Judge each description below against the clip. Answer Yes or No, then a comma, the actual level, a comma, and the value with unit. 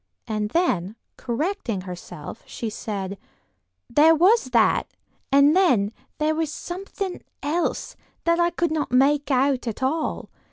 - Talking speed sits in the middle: No, slow, 130 wpm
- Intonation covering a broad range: Yes, wide, 7.0 semitones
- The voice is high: Yes, very high, 280 Hz